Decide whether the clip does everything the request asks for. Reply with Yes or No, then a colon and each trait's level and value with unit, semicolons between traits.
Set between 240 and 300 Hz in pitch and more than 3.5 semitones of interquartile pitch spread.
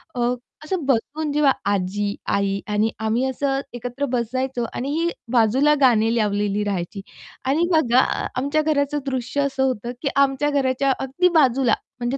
Yes: very high, 260 Hz; average, 3.9 semitones